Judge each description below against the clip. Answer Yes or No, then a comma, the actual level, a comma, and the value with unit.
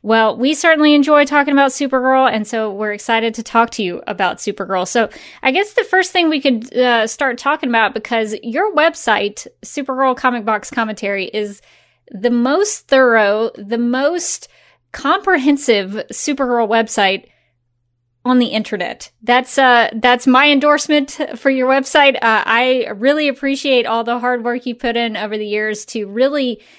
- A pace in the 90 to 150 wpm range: No, average, 160 wpm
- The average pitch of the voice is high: Yes, high, 245 Hz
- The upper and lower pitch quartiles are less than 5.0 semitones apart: Yes, average, 4.0 semitones